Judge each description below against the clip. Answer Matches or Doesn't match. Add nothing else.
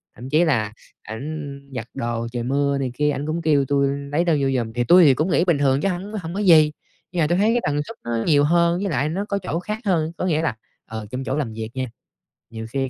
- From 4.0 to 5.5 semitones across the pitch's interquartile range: Matches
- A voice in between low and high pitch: Matches